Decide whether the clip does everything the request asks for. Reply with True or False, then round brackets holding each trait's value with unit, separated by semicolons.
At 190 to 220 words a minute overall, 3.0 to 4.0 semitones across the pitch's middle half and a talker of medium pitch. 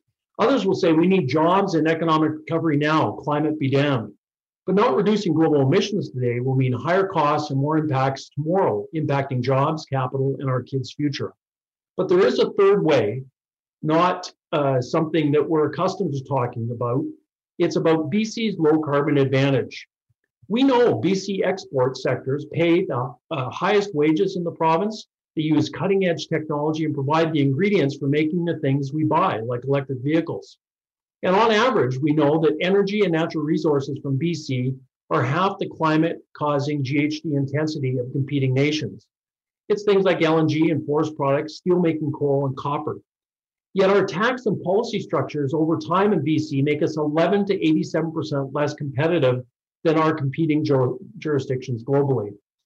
False (165 wpm; 3.5 semitones; 155 Hz)